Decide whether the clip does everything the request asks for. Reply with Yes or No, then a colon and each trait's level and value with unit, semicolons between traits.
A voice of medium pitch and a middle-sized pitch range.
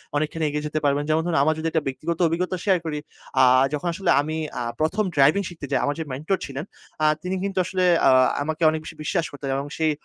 Yes: medium, 155 Hz; average, 3.2 semitones